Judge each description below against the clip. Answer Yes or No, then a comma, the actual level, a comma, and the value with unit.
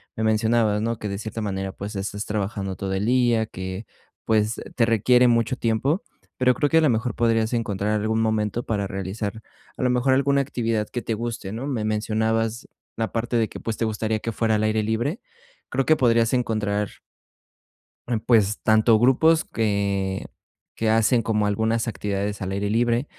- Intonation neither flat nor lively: No, narrow, 2.2 semitones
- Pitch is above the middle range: No, low, 110 Hz